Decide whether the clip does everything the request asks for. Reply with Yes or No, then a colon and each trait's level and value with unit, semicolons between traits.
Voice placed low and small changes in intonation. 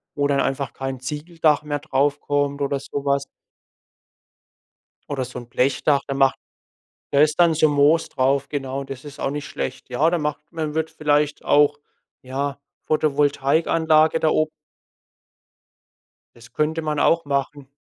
No: medium, 145 Hz; narrow, 1.8 semitones